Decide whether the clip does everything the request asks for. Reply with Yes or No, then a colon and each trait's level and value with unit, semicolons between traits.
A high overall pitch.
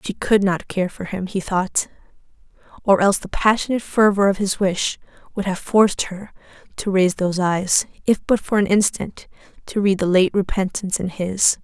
Yes: high, 195 Hz